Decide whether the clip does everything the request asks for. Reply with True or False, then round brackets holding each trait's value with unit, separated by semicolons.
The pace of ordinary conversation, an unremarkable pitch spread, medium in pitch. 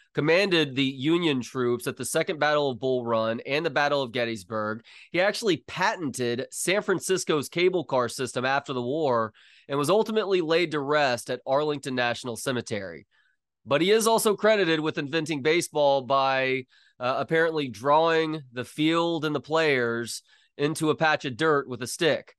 True (165 wpm; 4.3 semitones; 145 Hz)